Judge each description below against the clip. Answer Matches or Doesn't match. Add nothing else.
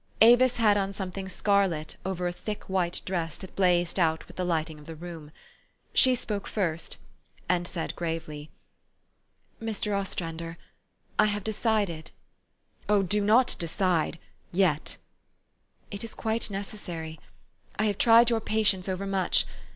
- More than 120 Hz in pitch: Matches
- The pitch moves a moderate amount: Matches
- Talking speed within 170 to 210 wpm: Doesn't match